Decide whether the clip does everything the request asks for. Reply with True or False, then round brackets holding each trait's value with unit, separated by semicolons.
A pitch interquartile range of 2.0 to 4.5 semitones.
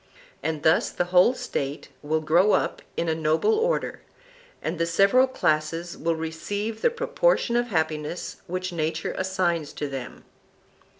True (4.0 semitones)